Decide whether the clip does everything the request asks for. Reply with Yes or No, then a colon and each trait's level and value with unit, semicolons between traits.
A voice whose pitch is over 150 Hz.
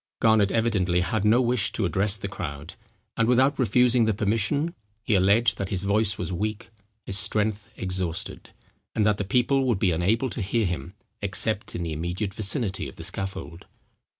No: low, 105 Hz